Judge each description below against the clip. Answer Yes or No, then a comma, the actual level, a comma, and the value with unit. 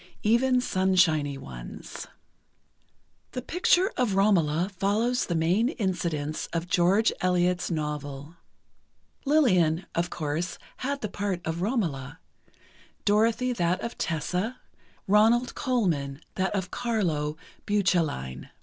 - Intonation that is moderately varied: No, wide, 5.7 semitones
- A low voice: No, medium, 185 Hz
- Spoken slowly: Yes, slow, 105 wpm